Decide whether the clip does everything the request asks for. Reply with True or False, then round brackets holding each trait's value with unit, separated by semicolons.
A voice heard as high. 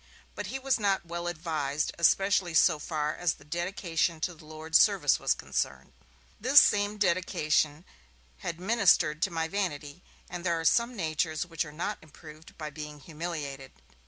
False (165 Hz)